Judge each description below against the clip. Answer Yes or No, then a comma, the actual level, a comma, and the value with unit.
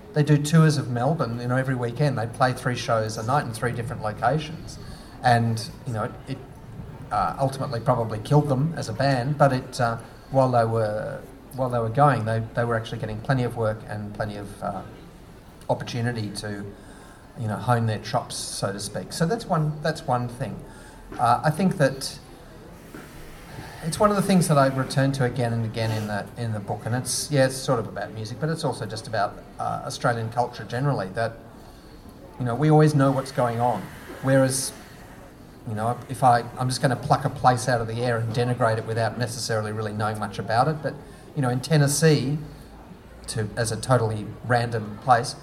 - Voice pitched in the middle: No, low, 125 Hz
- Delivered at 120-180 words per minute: No, average, 200 wpm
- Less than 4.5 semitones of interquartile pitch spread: Yes, average, 3.7 semitones